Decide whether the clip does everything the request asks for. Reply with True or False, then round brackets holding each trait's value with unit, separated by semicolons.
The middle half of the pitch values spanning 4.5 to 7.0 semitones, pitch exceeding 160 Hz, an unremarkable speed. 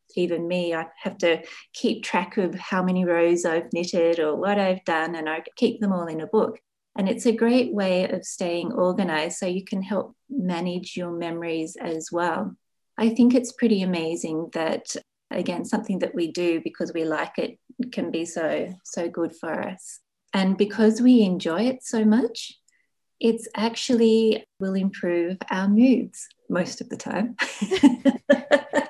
True (5.1 semitones; 190 Hz; 170 wpm)